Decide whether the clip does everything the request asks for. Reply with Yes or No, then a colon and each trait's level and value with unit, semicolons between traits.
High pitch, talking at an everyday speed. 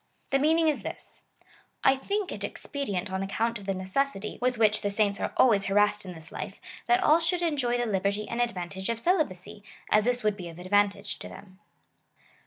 No: high, 210 Hz; fast, 210 wpm